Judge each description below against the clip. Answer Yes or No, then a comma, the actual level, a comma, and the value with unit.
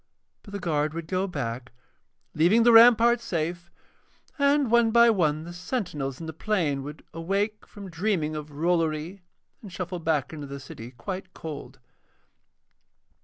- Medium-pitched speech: Yes, medium, 170 Hz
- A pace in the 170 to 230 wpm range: No, average, 150 wpm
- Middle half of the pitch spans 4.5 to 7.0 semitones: Yes, average, 5.2 semitones